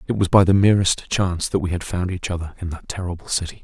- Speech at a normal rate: No, fast, 265 wpm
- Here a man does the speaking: Yes, male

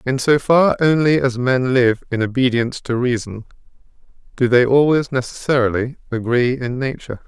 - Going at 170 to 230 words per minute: No, average, 150 wpm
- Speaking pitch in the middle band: No, low, 125 Hz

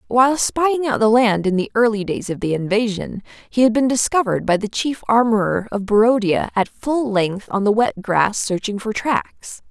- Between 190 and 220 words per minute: Yes, average, 200 wpm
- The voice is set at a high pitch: Yes, high, 220 Hz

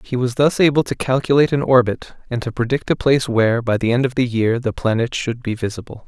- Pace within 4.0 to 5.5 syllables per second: No, 6.2 syllables/s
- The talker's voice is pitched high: No, low, 125 Hz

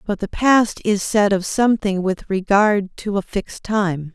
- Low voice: No, high, 200 Hz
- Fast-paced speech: No, average, 190 wpm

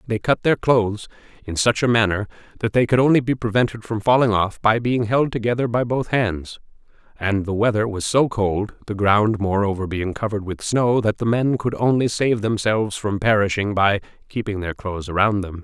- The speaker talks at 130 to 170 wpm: No, average, 190 wpm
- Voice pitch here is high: No, low, 110 Hz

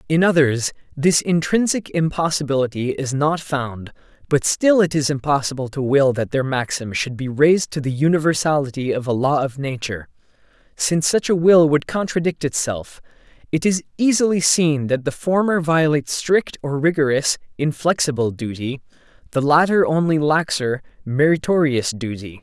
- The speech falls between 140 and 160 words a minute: Yes, average, 145 wpm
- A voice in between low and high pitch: Yes, medium, 145 Hz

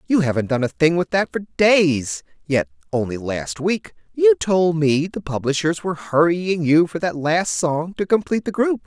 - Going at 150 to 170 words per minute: No, average, 195 wpm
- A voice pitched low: No, medium, 165 Hz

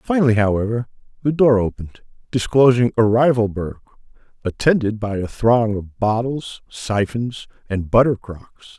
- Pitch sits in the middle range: No, low, 115 Hz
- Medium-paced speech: No, slow, 130 wpm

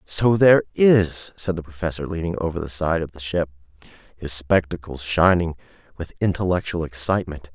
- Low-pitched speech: Yes, very low, 85 Hz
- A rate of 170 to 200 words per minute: No, average, 150 wpm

